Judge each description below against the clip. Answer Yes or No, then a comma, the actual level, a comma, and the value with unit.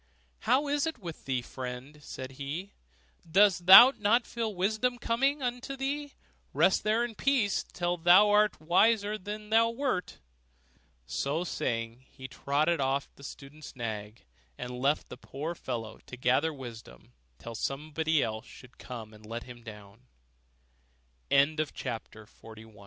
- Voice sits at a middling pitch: Yes, medium, 160 Hz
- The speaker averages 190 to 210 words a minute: No, average, 140 wpm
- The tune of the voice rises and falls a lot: Yes, wide, 8.9 semitones